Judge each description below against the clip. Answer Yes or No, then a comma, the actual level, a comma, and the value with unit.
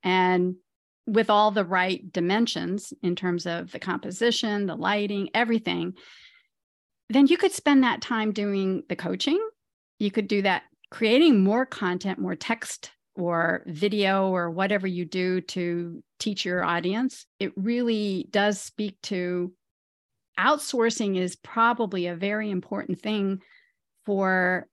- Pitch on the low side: No, high, 200 Hz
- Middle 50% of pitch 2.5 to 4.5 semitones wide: Yes, average, 3.6 semitones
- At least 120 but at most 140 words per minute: Yes, slow, 135 wpm